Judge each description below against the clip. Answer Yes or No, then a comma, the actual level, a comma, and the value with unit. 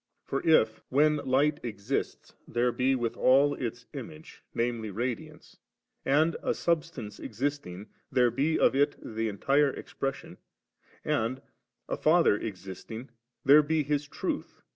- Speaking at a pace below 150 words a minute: Yes, average, 140 wpm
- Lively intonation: No, average, 4.3 semitones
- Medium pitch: No, low, 130 Hz